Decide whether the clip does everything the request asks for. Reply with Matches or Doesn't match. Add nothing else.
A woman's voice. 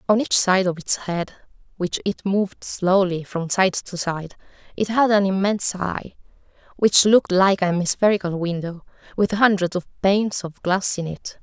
Matches